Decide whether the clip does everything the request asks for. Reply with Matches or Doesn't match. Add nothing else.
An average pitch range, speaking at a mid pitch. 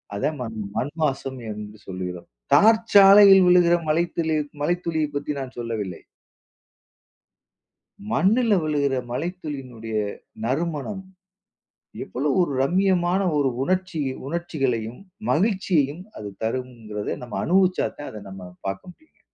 Doesn't match